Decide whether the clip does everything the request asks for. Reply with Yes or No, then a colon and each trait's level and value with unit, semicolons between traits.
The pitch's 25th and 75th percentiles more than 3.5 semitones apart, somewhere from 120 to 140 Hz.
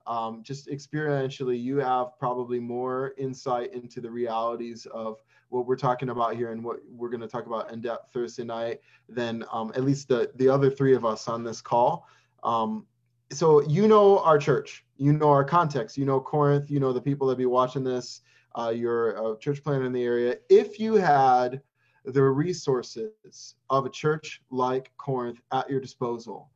No: narrow, 2.6 semitones; low, 130 Hz